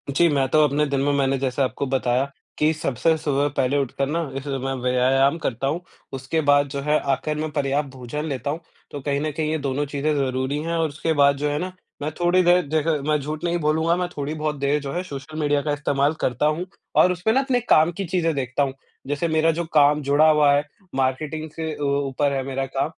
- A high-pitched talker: No, medium, 145 Hz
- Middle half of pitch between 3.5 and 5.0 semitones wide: No, narrow, 2.4 semitones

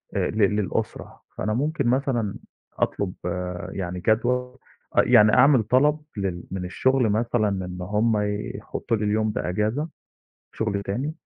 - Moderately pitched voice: No, low, 110 Hz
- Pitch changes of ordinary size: Yes, average, 4.1 semitones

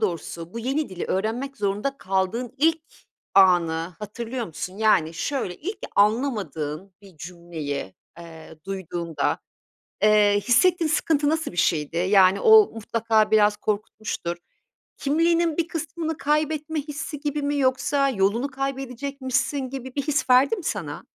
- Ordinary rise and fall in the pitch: No, wide, 7.2 semitones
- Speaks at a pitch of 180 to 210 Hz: No, high, 230 Hz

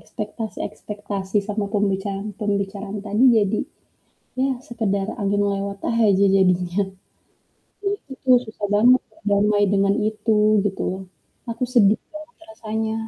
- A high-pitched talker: Yes, high, 205 Hz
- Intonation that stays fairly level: Yes, narrow, 1.9 semitones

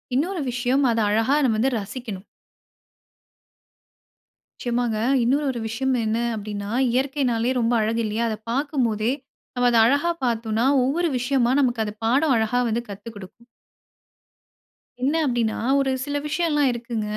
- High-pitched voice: Yes, high, 240 Hz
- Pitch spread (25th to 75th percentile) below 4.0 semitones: Yes, average, 3.3 semitones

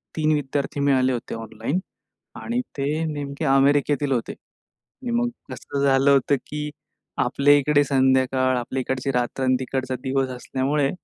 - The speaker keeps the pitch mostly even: Yes, narrow, 1.8 semitones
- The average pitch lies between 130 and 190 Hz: Yes, low, 135 Hz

